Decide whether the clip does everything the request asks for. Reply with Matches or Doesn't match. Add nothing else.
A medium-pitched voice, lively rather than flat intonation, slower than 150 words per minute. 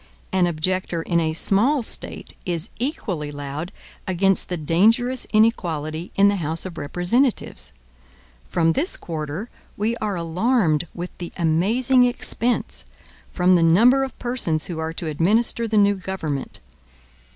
Matches